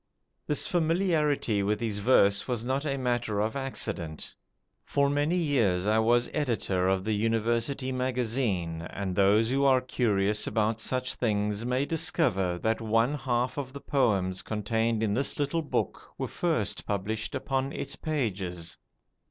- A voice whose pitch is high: No, low, 115 Hz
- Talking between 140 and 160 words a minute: Yes, average, 150 wpm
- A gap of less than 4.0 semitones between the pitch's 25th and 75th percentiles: No, average, 4.7 semitones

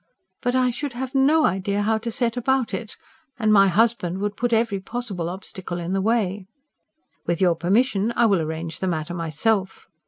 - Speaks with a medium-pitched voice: No, high, 205 Hz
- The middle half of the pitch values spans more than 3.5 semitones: Yes, average, 4.5 semitones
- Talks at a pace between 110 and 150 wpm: No, average, 185 wpm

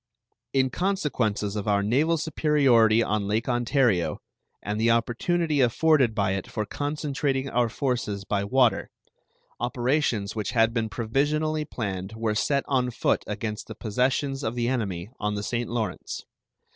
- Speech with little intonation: No, average, 4.4 semitones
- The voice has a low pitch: Yes, low, 120 Hz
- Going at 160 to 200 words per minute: No, average, 145 wpm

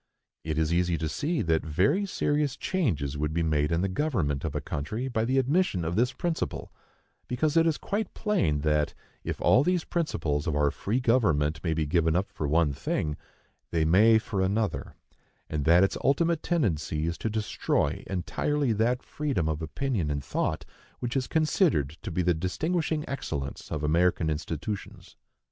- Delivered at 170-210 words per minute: Yes, average, 175 wpm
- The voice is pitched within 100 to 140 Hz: No, very low, 90 Hz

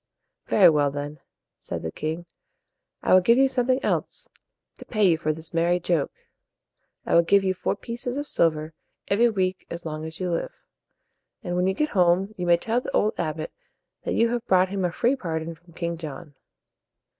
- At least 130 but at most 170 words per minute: No, average, 195 wpm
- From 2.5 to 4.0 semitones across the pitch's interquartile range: No, average, 4.6 semitones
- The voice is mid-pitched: Yes, medium, 175 Hz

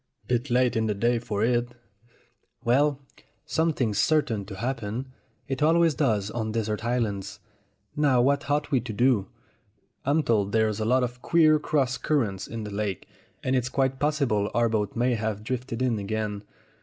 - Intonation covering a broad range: No, average, 3.8 semitones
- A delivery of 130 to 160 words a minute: No, average, 170 wpm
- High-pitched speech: No, low, 120 Hz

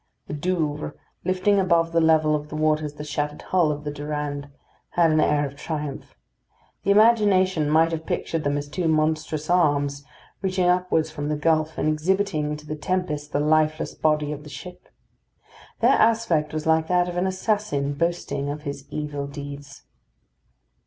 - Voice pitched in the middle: Yes, medium, 155 Hz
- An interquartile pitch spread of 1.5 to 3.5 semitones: Yes, average, 3.0 semitones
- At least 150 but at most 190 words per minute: Yes, average, 170 wpm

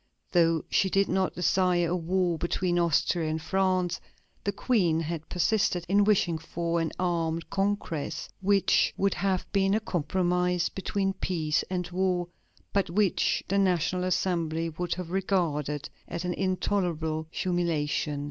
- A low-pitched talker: No, medium, 180 Hz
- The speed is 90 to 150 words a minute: Yes, average, 140 wpm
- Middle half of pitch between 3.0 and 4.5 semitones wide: No, narrow, 2.4 semitones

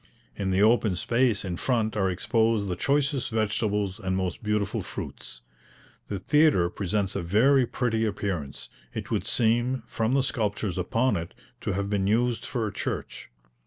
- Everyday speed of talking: Yes, average, 160 wpm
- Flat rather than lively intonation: No, average, 3.8 semitones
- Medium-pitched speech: No, low, 105 Hz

